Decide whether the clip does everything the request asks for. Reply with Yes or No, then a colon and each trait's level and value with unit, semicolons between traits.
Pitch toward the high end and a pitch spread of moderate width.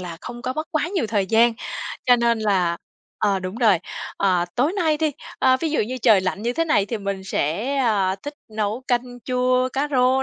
Yes: high, 240 Hz; average, 4.5 semitones